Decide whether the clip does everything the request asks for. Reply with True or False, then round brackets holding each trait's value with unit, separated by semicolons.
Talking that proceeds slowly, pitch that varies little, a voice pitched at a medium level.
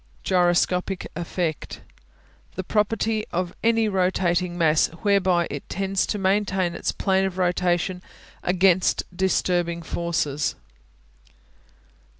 True (100 wpm; 1.9 semitones; 180 Hz)